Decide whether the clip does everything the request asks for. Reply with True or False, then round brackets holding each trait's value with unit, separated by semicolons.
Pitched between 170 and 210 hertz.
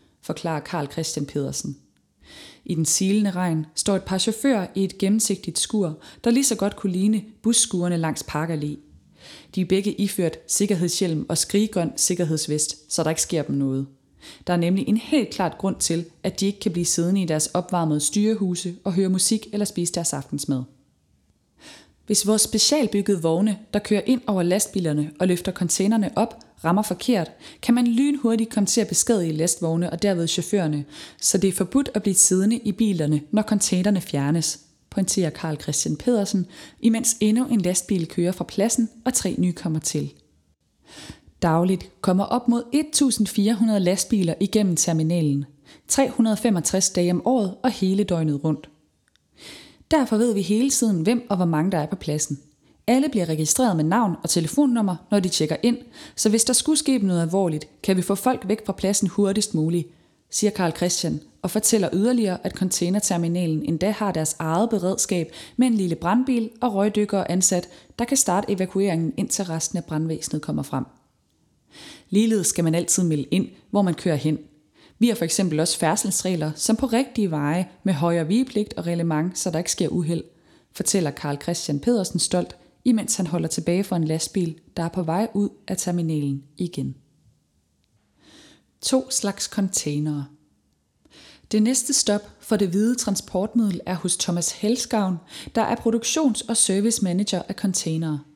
True (190 Hz)